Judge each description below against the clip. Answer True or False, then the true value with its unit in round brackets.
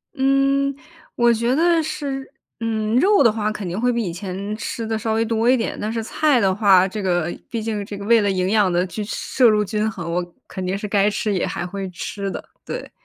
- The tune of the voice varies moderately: True (3.3 semitones)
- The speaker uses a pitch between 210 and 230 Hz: True (215 Hz)